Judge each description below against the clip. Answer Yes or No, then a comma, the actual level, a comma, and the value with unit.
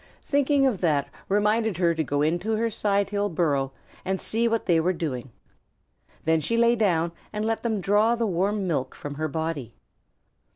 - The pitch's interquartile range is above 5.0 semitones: Yes, wide, 5.5 semitones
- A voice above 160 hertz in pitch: Yes, high, 190 Hz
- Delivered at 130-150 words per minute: No, average, 175 wpm